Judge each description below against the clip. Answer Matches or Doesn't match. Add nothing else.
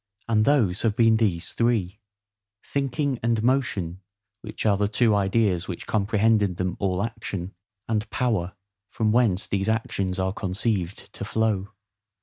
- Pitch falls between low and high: Doesn't match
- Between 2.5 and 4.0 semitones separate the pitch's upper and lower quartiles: Matches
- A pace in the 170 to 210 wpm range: Doesn't match